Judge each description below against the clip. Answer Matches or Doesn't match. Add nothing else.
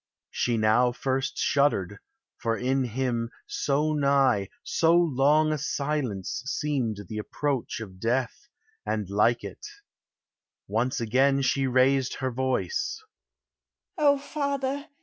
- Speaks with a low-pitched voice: Matches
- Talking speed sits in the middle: Doesn't match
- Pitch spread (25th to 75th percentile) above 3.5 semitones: Matches